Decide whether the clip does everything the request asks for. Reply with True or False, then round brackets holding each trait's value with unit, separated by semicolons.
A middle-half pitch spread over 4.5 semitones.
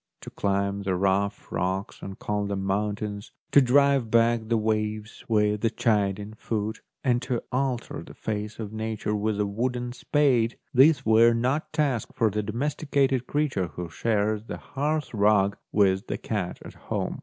False (3.2 semitones)